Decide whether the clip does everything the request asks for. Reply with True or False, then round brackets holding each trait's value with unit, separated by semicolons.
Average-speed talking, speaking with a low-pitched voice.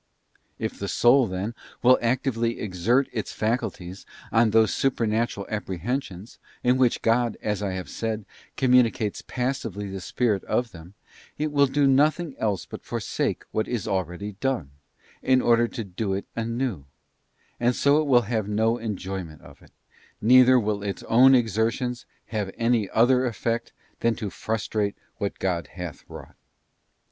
True (150 wpm; 115 Hz)